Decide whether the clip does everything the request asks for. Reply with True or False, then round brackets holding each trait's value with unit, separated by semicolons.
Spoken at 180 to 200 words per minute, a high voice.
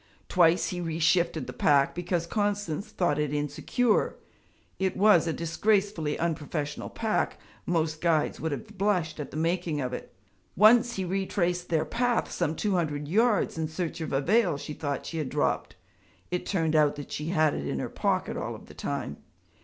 False (185 wpm; 170 Hz)